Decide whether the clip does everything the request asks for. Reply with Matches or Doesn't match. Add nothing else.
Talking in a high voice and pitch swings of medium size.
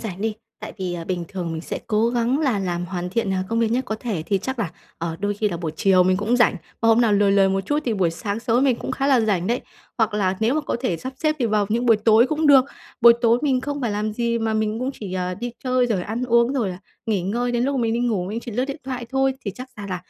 Matches